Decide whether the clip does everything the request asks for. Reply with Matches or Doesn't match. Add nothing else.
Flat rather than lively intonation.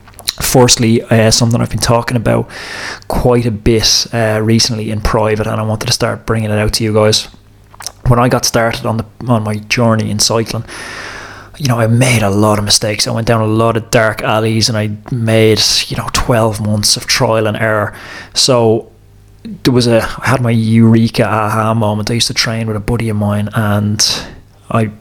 Matches